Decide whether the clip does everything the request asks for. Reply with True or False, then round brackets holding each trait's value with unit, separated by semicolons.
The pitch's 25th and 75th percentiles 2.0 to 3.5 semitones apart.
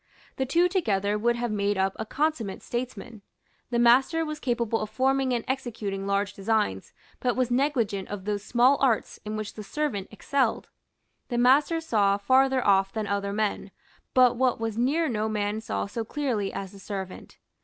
False (4.3 semitones)